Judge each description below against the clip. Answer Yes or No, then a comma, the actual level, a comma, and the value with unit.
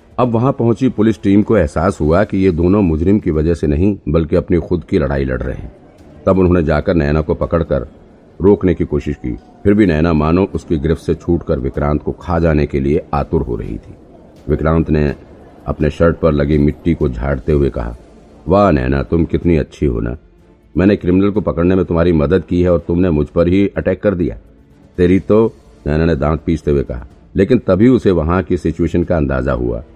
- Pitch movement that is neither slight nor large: Yes, average, 4.1 semitones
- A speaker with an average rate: No, fast, 210 wpm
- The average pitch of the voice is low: Yes, very low, 85 Hz